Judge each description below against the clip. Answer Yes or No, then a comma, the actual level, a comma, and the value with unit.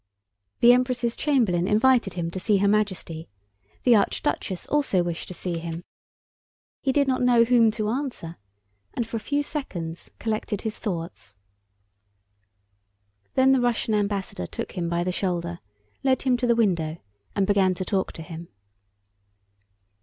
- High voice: Yes, high, 205 Hz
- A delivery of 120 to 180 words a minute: Yes, average, 155 wpm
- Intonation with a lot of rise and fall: Yes, wide, 5.8 semitones